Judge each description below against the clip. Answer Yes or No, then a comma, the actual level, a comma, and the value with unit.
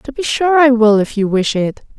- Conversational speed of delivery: No, fast, 270 wpm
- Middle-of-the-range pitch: No, high, 245 Hz